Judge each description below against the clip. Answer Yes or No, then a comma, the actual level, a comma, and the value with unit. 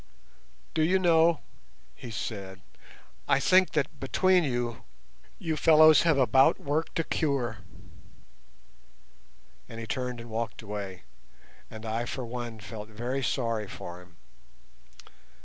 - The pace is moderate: No, slow, 125 wpm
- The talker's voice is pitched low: Yes, low, 120 Hz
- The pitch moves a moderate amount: No, wide, 5.9 semitones